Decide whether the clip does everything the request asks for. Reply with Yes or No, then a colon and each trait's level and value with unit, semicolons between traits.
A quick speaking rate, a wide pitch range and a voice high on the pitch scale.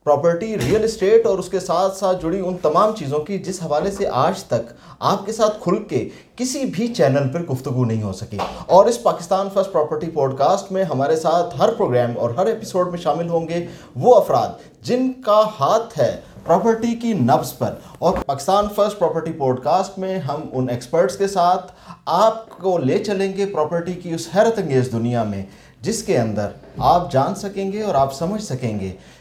No: fast, 195 wpm; wide, 6.2 semitones; medium, 175 Hz